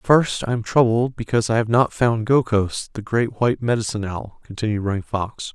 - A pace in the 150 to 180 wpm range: No, average, 195 wpm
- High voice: No, low, 115 Hz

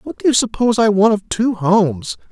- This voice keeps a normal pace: No, fast, 235 wpm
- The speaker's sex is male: Yes, male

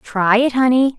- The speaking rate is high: No, average, 180 wpm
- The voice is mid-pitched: No, high, 240 Hz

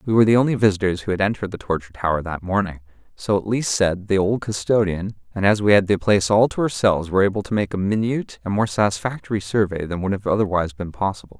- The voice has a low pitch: Yes, low, 100 Hz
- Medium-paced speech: No, fast, 225 wpm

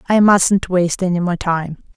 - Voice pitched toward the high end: No, medium, 180 Hz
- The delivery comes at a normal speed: Yes, average, 185 wpm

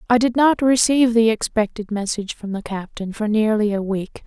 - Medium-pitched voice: No, high, 220 Hz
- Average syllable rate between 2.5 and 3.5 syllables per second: No, 5.4 syllables/s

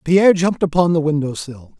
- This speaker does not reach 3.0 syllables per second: No, 6.1 syllables/s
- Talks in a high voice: No, medium, 160 Hz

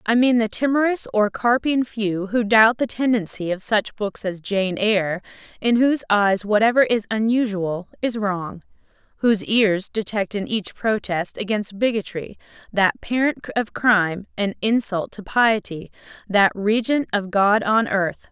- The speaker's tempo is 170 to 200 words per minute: No, average, 145 wpm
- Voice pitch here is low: No, high, 210 Hz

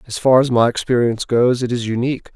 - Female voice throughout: No, male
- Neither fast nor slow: No, fast, 230 wpm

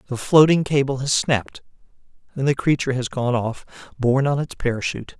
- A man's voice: Yes, male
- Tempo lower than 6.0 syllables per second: No, 6.1 syllables/s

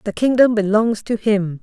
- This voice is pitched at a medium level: No, high, 215 Hz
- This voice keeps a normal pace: Yes, average, 185 wpm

